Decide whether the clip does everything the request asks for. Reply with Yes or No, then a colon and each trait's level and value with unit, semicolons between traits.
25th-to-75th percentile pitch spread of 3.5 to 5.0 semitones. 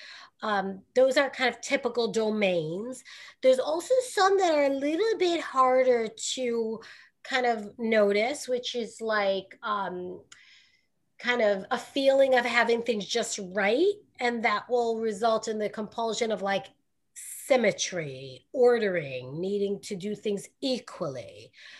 Yes: average, 4.1 semitones